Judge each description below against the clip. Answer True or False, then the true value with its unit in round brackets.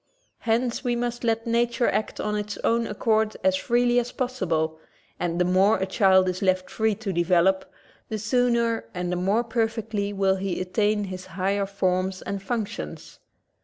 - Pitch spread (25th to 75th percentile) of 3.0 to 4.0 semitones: True (3.7 semitones)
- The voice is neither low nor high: False (210 Hz)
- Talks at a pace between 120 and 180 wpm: True (165 wpm)